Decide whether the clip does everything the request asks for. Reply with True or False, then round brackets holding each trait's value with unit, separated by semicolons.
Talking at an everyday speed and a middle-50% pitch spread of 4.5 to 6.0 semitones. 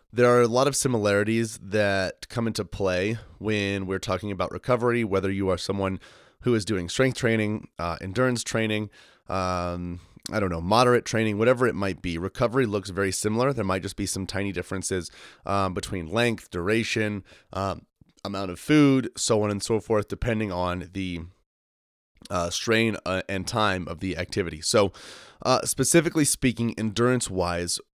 False (165 wpm; 3.7 semitones)